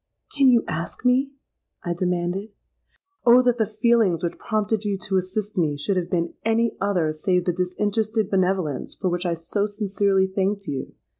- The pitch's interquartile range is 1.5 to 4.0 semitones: Yes, average, 3.5 semitones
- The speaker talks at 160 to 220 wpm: Yes, average, 170 wpm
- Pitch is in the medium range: No, high, 195 Hz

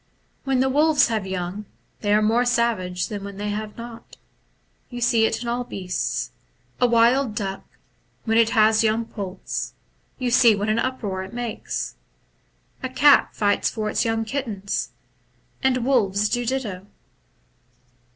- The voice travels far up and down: No, average, 3.0 semitones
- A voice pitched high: Yes, high, 225 Hz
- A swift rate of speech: No, average, 160 wpm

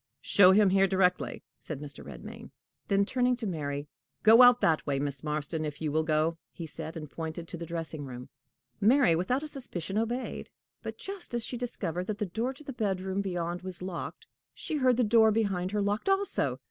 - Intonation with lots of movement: Yes, wide, 6.0 semitones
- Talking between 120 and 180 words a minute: No, average, 200 wpm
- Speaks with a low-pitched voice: No, medium, 185 Hz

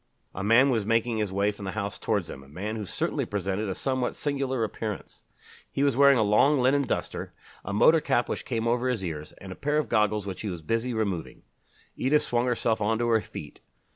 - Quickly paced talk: Yes, fast, 225 wpm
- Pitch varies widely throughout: No, average, 4.0 semitones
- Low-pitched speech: Yes, low, 110 Hz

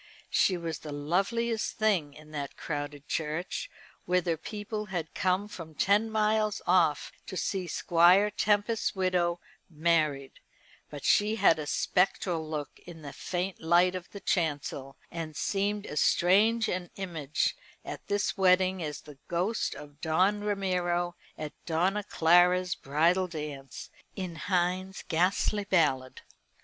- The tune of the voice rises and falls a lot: No, average, 3.9 semitones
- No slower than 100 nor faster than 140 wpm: Yes, slow, 135 wpm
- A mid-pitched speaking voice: Yes, medium, 175 Hz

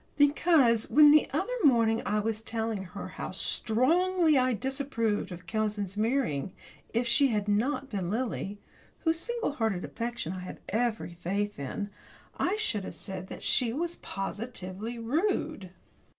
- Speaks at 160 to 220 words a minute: No, average, 150 wpm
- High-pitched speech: Yes, high, 230 Hz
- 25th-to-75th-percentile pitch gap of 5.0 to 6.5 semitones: Yes, wide, 5.5 semitones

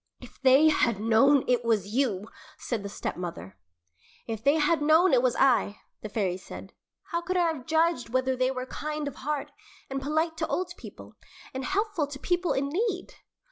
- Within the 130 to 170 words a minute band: No, average, 190 wpm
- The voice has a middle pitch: No, very high, 275 Hz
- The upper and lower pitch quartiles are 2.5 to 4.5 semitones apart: No, wide, 5.4 semitones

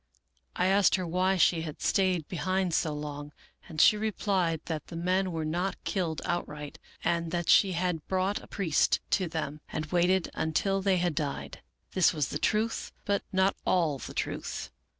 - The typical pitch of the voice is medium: Yes, medium, 175 Hz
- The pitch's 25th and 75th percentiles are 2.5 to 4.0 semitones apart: Yes, average, 3.1 semitones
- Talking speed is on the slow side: No, average, 175 wpm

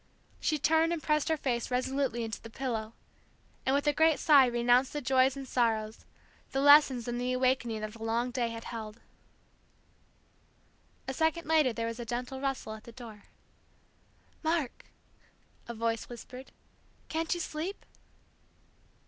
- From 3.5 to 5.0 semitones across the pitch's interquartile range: Yes, average, 3.8 semitones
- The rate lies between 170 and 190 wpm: No, average, 155 wpm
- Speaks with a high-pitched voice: Yes, very high, 255 Hz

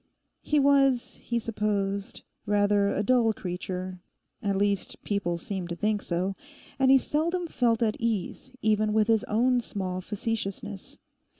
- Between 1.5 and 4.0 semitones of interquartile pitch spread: Yes, average, 3.4 semitones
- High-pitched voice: Yes, high, 210 Hz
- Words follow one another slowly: Yes, slow, 130 wpm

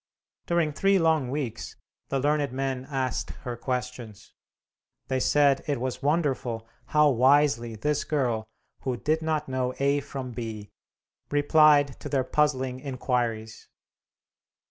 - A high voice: No, low, 135 Hz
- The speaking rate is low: Yes, slow, 125 wpm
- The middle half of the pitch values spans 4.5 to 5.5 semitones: No, average, 2.9 semitones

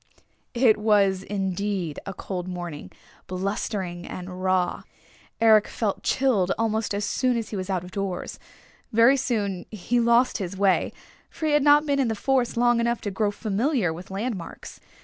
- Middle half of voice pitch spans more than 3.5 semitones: Yes, average, 4.1 semitones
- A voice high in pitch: Yes, high, 205 Hz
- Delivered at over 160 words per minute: Yes, average, 170 wpm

